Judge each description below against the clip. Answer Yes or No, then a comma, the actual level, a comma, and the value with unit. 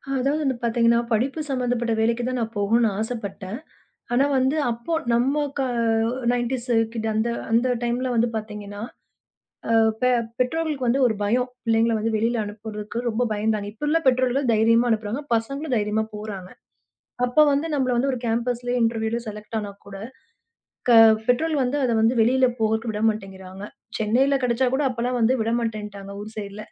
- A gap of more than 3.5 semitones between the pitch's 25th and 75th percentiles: No, average, 2.7 semitones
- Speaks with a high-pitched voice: Yes, high, 235 Hz